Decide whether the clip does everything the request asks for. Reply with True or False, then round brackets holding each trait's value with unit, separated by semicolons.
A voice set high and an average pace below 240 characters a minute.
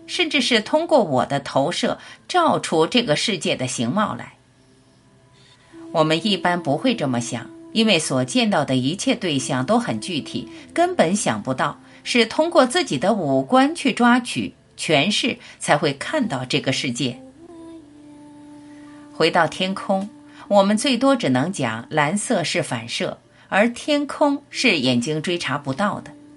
True (215 Hz; 215 characters per minute)